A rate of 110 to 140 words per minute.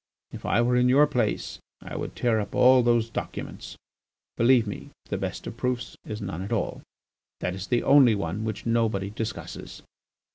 No: average, 180 wpm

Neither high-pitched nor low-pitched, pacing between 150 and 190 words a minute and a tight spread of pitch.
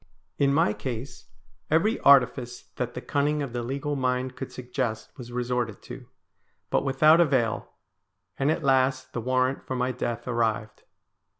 No: low, 130 Hz; average, 155 wpm; narrow, 2.2 semitones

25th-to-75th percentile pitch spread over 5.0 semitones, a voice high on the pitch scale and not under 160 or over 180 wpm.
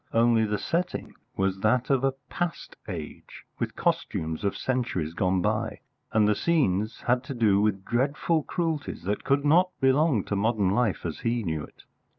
No: wide, 5.6 semitones; low, 115 Hz; average, 170 wpm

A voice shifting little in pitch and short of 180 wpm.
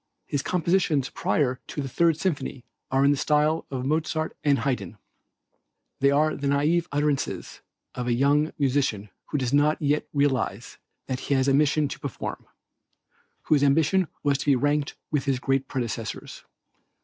Yes: narrow, 2.3 semitones; average, 160 wpm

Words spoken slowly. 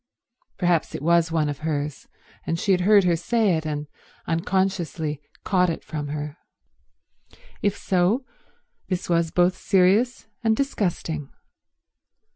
Yes: slow, 130 wpm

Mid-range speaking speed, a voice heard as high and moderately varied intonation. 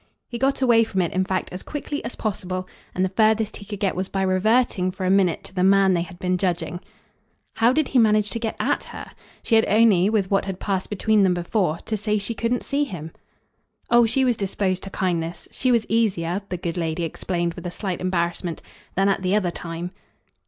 No: fast, 225 wpm; high, 195 Hz; average, 3.4 semitones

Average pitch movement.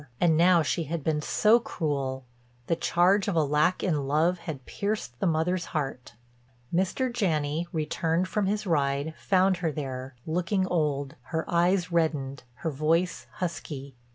Yes: average, 3.7 semitones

